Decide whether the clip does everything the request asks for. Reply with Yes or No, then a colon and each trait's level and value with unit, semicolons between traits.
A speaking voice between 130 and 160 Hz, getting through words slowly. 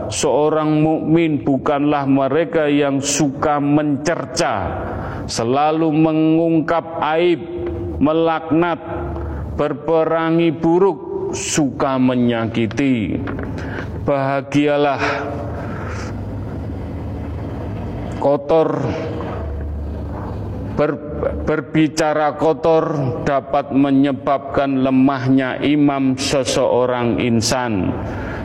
Yes: medium, 140 Hz; slow, 55 wpm